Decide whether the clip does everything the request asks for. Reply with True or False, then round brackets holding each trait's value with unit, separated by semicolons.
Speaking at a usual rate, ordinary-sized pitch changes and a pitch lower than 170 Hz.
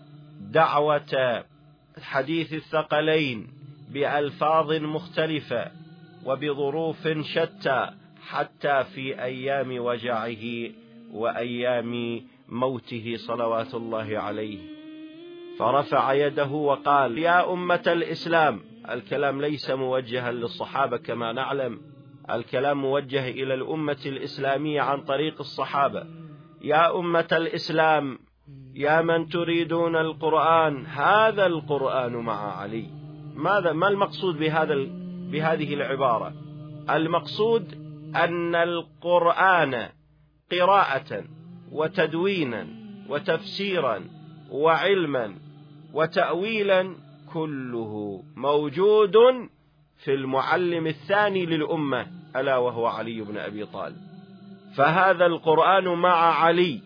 True (80 wpm; 3.7 semitones; 150 Hz)